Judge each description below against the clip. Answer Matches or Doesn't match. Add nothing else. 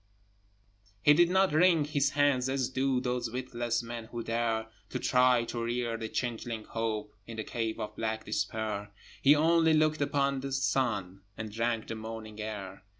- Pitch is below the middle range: Matches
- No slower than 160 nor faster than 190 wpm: Matches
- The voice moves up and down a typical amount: Matches